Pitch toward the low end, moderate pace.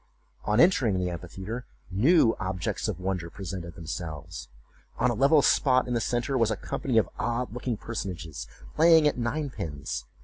Yes: low, 110 Hz; average, 165 wpm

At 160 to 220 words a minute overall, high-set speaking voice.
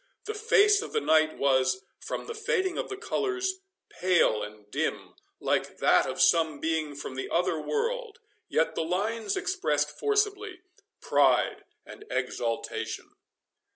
No: average, 140 wpm; very high, 345 Hz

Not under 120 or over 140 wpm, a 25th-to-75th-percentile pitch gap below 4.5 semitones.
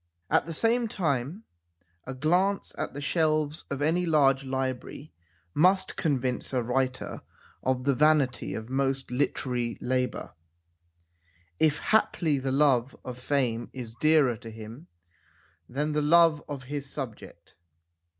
Yes: slow, 135 wpm; average, 3.4 semitones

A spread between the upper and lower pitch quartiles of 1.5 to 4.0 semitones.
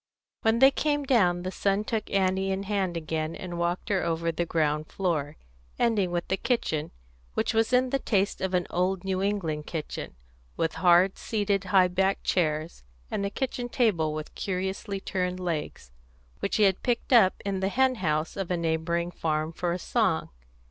Yes: average, 3.2 semitones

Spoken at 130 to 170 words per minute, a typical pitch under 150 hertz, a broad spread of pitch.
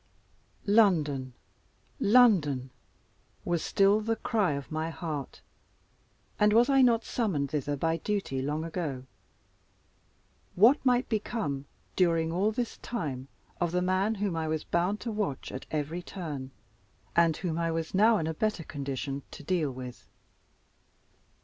No: average, 140 wpm; medium, 170 Hz; wide, 6.1 semitones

